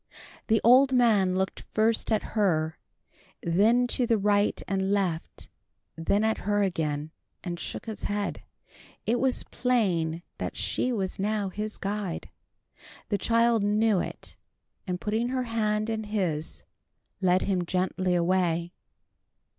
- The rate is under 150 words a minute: Yes, slow, 135 wpm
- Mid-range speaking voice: No, high, 205 Hz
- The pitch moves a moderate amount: Yes, average, 3.5 semitones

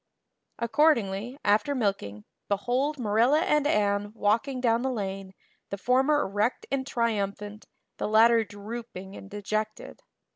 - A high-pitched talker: Yes, high, 220 Hz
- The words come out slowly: Yes, slow, 120 wpm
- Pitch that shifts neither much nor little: Yes, average, 3.8 semitones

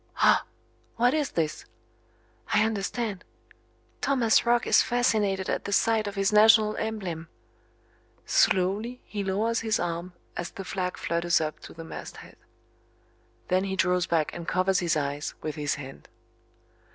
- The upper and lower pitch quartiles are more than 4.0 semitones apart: Yes, average, 4.4 semitones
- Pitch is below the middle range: No, high, 195 Hz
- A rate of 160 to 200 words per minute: No, average, 150 wpm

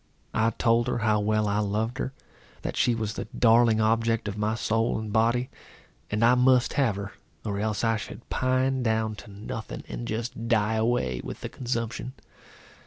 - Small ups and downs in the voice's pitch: Yes, narrow, 1.8 semitones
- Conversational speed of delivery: Yes, average, 180 wpm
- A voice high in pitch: No, low, 115 Hz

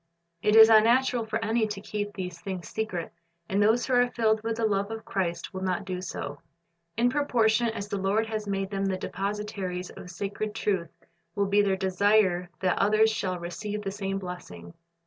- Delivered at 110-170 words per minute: No, average, 190 wpm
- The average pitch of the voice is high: Yes, high, 205 Hz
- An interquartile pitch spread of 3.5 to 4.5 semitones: No, narrow, 2.6 semitones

